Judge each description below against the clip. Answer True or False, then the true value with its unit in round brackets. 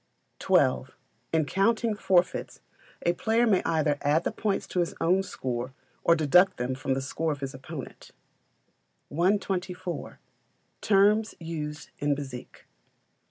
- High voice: False (165 Hz)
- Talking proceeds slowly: True (130 wpm)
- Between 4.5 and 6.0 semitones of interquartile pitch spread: True (5.1 semitones)